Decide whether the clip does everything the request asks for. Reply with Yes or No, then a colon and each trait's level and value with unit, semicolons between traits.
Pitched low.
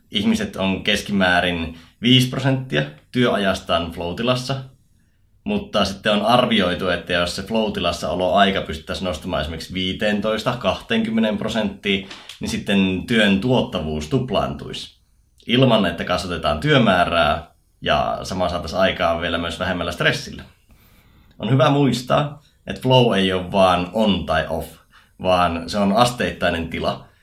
Yes: very low, 95 Hz